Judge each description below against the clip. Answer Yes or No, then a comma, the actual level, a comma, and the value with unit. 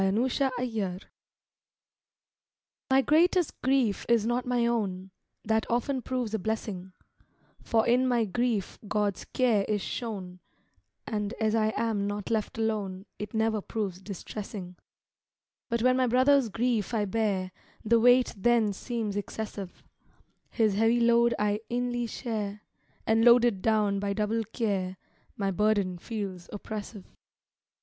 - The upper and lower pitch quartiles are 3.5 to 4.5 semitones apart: No, average, 2.9 semitones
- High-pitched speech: Yes, high, 220 Hz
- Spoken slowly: Yes, slow, 130 wpm